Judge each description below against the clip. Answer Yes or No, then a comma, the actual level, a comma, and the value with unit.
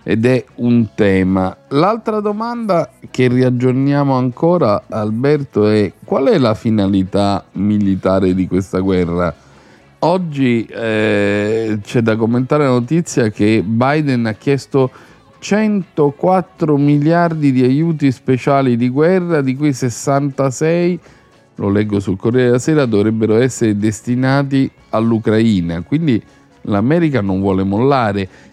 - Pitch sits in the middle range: No, low, 125 Hz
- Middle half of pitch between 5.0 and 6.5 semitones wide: Yes, wide, 5.4 semitones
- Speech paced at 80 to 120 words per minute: Yes, slow, 115 wpm